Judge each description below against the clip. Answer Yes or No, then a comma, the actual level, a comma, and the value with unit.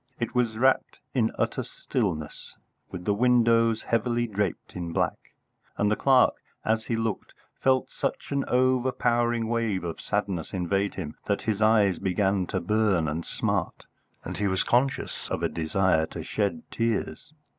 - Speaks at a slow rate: No, average, 155 wpm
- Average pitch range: Yes, average, 3.8 semitones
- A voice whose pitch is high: No, low, 110 Hz